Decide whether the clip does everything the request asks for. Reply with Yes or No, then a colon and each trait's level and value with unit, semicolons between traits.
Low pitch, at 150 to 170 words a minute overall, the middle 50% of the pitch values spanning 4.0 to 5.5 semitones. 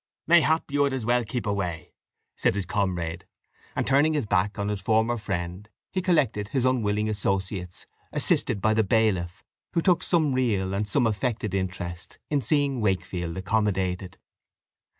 Yes: low, 105 Hz; average, 155 wpm; average, 5.2 semitones